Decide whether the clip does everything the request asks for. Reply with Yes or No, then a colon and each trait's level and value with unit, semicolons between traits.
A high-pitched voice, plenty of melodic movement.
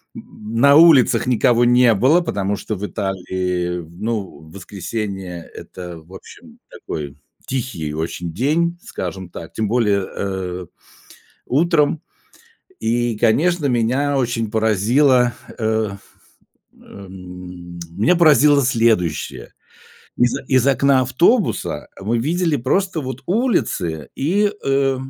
No: low, 115 Hz; wide, 6.6 semitones